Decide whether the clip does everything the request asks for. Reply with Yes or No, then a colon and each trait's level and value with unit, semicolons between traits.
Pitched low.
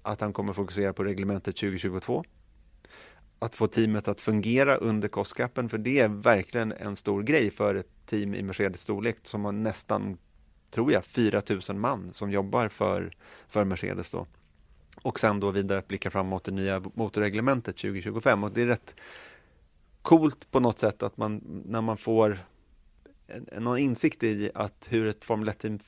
Yes: low, 105 Hz